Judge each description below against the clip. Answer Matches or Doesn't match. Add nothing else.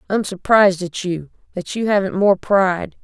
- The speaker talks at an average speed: Matches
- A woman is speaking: Matches